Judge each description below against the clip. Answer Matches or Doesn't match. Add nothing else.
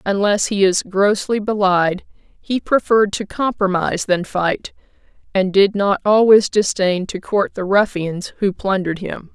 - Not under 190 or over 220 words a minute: Doesn't match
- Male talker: Doesn't match